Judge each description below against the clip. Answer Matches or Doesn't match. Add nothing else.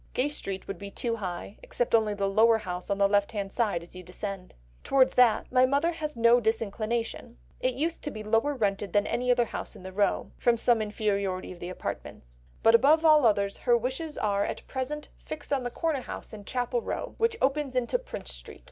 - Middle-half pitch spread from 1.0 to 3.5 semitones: Doesn't match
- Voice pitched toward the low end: Doesn't match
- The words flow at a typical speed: Doesn't match